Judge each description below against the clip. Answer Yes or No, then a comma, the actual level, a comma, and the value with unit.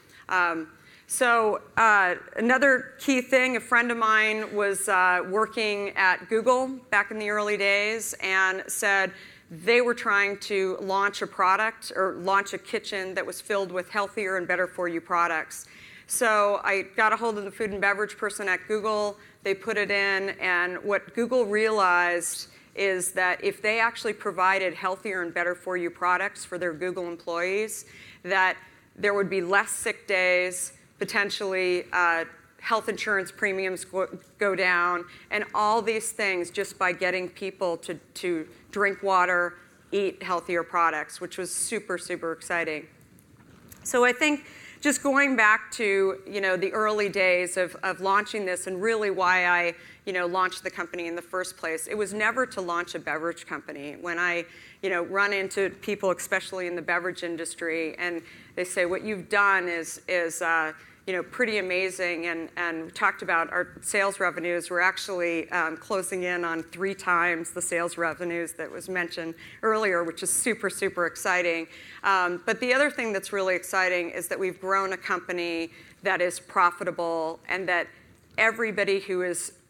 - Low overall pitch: No, medium, 185 Hz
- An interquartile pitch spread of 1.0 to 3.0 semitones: Yes, average, 2.7 semitones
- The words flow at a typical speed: Yes, average, 170 wpm